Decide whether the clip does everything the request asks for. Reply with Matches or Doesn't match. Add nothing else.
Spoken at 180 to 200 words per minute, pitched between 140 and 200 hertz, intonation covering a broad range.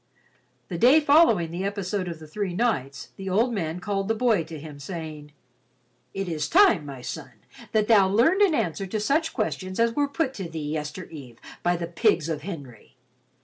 Matches